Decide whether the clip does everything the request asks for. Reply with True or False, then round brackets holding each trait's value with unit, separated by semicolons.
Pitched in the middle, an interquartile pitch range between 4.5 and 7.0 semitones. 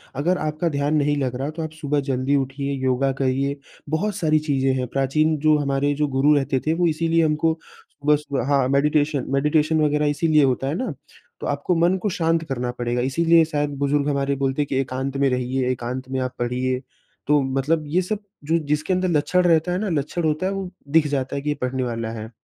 False (145 Hz; 2.9 semitones)